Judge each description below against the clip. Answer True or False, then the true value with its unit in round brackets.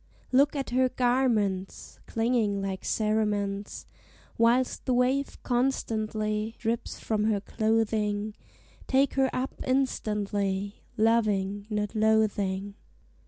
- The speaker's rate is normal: False (100 wpm)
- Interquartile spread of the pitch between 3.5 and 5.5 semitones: False (3.1 semitones)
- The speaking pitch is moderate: False (220 Hz)